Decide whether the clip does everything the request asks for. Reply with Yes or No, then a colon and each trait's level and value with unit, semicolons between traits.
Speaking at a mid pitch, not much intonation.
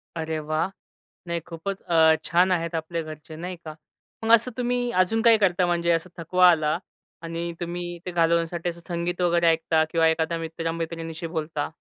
Yes: medium, 170 Hz; narrow, 1.5 semitones